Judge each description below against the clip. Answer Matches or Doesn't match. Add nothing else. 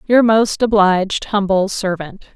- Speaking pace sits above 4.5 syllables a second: Doesn't match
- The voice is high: Matches